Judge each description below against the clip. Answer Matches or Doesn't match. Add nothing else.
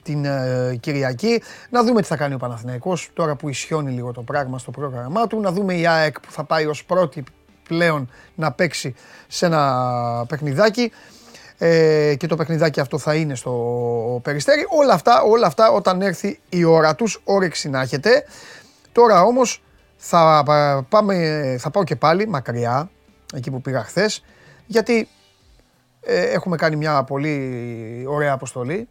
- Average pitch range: Doesn't match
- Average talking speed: Matches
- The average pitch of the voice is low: Doesn't match